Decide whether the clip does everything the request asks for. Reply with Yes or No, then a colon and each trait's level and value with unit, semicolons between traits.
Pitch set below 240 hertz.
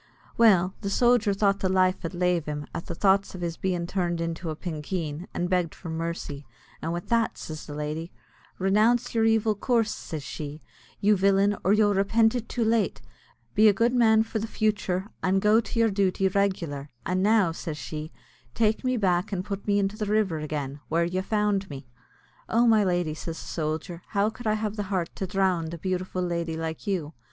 Yes: high, 190 Hz